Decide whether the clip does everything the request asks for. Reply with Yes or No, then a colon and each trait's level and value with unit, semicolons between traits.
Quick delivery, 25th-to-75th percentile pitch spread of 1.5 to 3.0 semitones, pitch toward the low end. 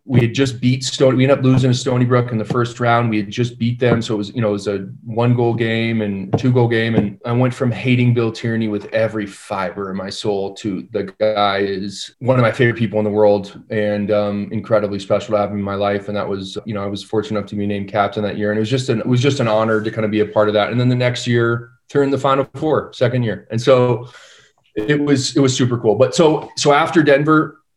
No: fast, 275 wpm; average, 3.4 semitones; low, 115 Hz